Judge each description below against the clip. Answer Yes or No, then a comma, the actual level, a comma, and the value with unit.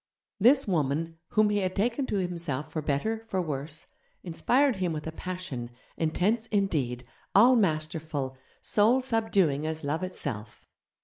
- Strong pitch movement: Yes, wide, 5.8 semitones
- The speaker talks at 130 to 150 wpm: Yes, average, 140 wpm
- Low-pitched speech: No, medium, 175 Hz